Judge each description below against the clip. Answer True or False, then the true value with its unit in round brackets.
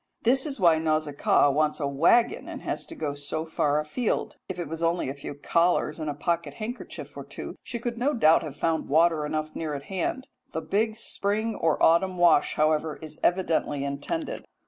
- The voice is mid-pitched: True (160 Hz)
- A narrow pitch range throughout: False (4.1 semitones)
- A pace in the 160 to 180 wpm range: False (195 wpm)